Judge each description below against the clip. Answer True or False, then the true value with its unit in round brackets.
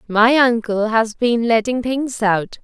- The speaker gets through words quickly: False (160 wpm)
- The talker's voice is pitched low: False (230 Hz)